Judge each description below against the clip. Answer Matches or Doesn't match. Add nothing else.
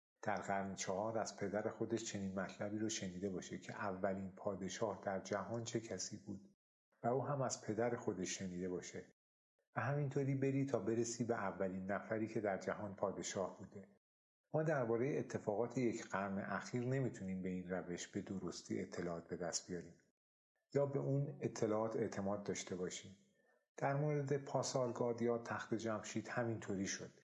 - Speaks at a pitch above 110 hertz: Doesn't match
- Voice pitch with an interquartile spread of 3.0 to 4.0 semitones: Matches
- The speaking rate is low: Doesn't match